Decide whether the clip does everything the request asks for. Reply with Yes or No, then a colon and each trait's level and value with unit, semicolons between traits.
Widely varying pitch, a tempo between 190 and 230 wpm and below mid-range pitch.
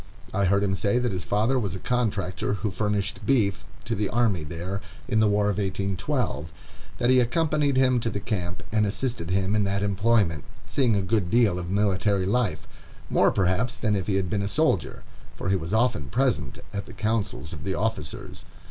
No: average, 3.6 semitones; average, 200 wpm; low, 100 Hz